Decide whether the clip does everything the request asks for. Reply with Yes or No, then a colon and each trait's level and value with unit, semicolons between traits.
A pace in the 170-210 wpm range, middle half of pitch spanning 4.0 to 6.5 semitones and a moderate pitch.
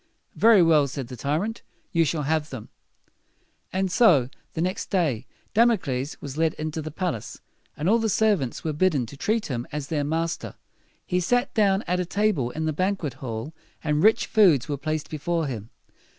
Yes: average, 180 wpm; average, 5.1 semitones; medium, 160 Hz